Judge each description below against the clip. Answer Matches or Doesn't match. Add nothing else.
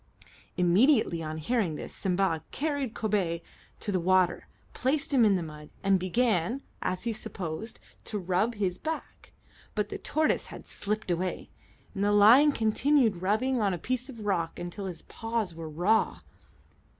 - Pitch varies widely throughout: Doesn't match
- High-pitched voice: Matches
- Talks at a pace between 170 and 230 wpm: Doesn't match